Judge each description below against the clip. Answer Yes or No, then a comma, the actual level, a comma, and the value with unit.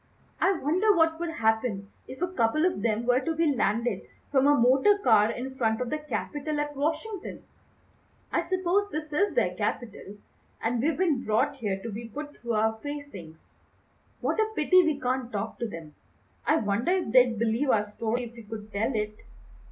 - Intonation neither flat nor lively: No, wide, 5.8 semitones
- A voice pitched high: Yes, very high, 255 Hz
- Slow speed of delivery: No, average, 190 wpm